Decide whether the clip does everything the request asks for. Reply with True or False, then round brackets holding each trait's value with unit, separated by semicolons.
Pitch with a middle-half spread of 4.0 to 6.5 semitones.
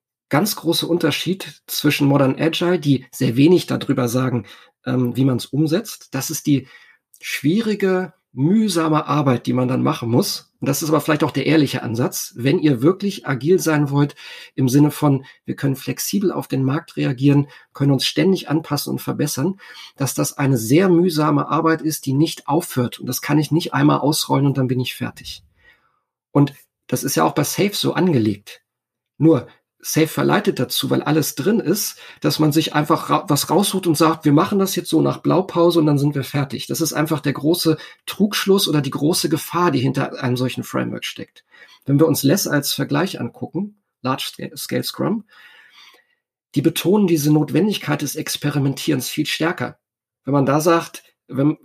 False (3.5 semitones)